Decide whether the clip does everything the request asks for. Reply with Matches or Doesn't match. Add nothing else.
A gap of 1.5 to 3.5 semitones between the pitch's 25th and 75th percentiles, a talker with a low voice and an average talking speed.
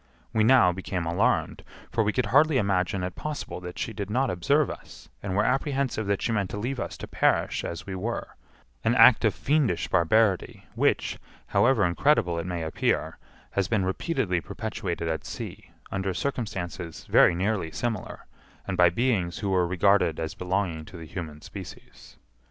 Doesn't match